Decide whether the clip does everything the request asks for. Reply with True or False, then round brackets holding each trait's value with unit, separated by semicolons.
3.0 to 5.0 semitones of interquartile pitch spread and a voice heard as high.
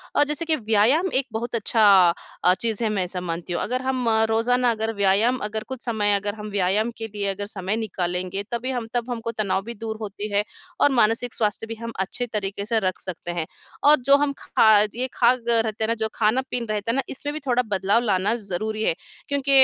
True (3.3 semitones; 220 Hz)